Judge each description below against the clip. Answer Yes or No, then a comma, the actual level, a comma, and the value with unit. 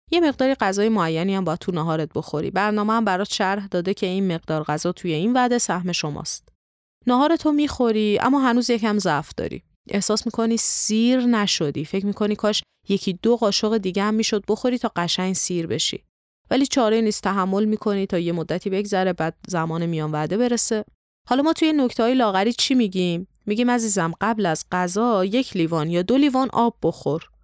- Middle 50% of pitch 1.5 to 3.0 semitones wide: No, average, 4.7 semitones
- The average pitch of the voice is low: No, high, 205 Hz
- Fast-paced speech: Yes, fast, 180 wpm